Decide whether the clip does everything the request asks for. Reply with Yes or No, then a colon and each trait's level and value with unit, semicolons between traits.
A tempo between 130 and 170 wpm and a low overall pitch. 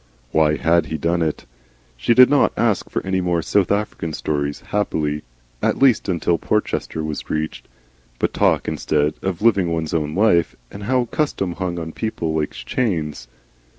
Yes: average, 165 wpm; very low, 85 Hz